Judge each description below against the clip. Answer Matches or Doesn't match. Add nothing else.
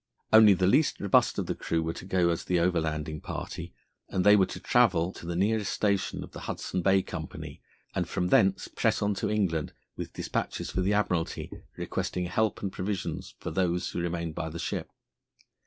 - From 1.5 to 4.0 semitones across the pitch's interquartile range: Matches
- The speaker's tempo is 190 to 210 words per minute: Matches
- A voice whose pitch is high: Doesn't match